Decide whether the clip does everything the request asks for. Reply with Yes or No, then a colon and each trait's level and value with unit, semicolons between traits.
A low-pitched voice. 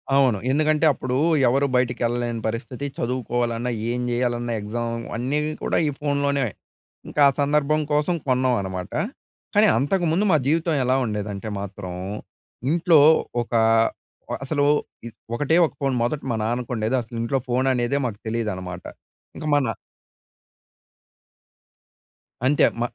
Yes: low, 125 Hz